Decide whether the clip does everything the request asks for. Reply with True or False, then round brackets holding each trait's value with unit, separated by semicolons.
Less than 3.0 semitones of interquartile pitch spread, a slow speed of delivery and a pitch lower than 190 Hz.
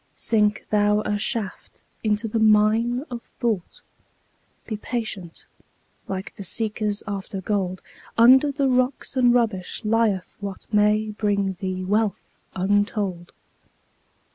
False (2.5 semitones; 115 wpm; 210 Hz)